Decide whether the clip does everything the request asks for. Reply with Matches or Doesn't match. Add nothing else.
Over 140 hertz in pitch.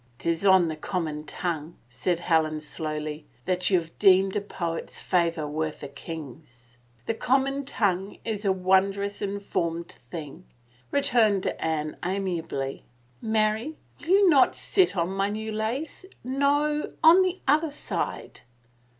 Matches